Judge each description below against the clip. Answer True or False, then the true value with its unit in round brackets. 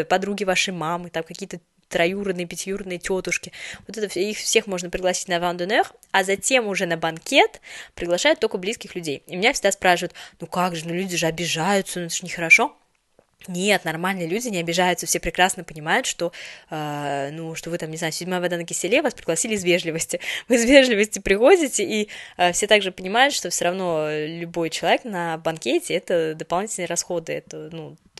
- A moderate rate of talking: False (185 wpm)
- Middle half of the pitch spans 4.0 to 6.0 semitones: False (2.6 semitones)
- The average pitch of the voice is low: False (180 Hz)